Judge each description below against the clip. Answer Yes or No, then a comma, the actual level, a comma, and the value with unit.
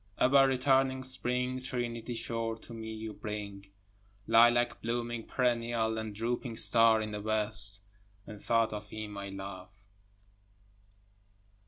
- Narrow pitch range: Yes, narrow, 2.2 semitones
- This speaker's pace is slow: Yes, slow, 125 wpm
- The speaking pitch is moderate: No, low, 115 Hz